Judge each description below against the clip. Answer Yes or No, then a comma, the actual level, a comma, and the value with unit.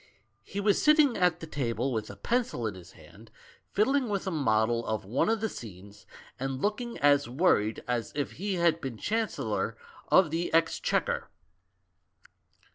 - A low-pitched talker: No, medium, 155 Hz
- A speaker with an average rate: Yes, average, 160 wpm